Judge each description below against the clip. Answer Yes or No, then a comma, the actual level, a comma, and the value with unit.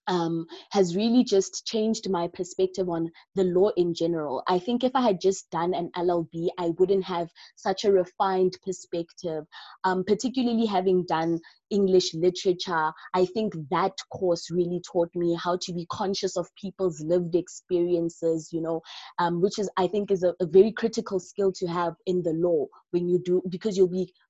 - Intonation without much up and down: Yes, narrow, 1.9 semitones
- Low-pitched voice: No, medium, 180 Hz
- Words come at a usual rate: Yes, average, 180 wpm